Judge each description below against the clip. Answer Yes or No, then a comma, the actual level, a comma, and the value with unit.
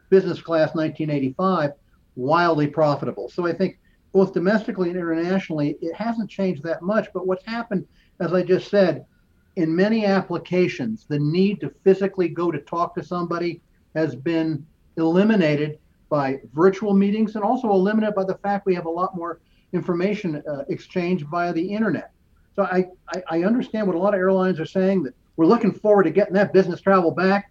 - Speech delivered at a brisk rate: No, average, 175 wpm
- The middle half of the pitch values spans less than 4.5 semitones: Yes, average, 3.0 semitones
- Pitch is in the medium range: Yes, medium, 180 Hz